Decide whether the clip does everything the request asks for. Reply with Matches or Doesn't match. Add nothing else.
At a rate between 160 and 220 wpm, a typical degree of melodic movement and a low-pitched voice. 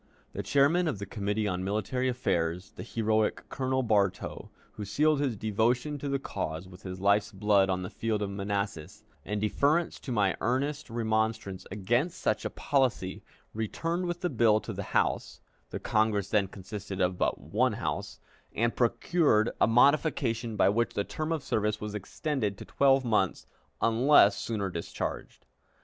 Matches